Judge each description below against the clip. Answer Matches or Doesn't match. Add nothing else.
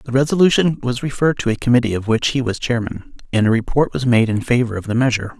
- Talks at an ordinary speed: Doesn't match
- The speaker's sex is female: Doesn't match